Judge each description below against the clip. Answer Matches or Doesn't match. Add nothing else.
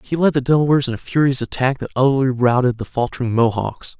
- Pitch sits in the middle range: Doesn't match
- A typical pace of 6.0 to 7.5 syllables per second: Matches